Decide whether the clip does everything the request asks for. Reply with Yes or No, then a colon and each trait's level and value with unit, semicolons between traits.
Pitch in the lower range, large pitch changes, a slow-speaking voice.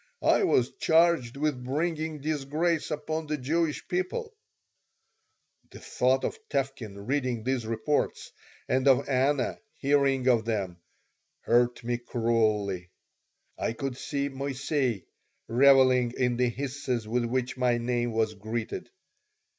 No: low, 130 Hz; average, 3.2 semitones; slow, 125 wpm